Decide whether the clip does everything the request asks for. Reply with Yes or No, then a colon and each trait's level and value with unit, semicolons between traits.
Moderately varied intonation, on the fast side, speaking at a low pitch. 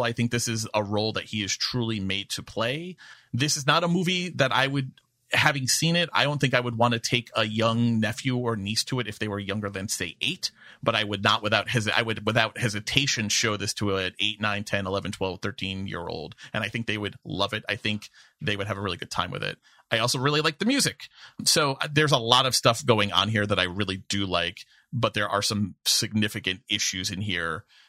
Yes: average, 3.6 semitones; fast, 245 wpm; low, 110 Hz